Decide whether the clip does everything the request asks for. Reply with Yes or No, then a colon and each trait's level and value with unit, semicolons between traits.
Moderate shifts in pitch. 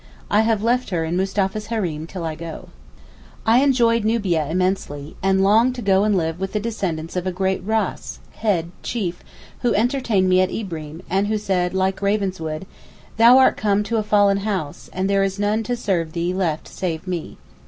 Yes: average, 3.4 semitones